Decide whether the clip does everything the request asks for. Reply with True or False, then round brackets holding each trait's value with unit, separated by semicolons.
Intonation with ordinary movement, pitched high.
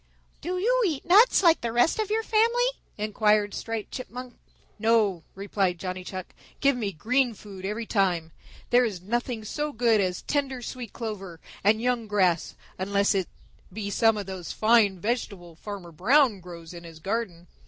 True (4.7 semitones; 215 Hz)